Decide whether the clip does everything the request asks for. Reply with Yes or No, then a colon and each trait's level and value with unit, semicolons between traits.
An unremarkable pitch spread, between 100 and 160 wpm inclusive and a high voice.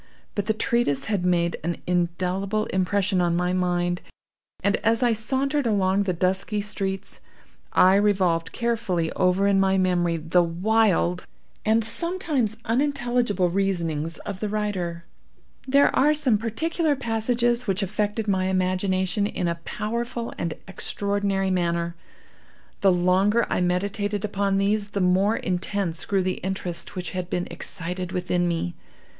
Yes: average, 3.2 semitones; average, 140 wpm; high, 195 Hz